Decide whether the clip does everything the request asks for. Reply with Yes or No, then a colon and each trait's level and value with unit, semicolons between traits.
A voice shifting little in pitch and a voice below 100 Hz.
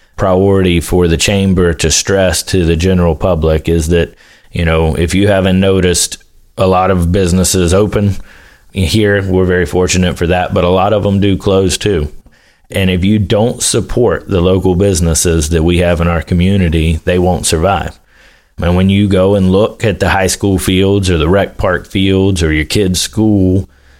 Yes: narrow, 2.1 semitones; very low, 90 Hz